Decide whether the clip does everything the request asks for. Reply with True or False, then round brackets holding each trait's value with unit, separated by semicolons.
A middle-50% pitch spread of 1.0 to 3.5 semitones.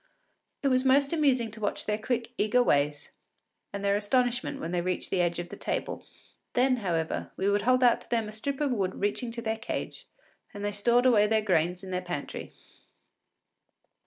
False (4.9 semitones)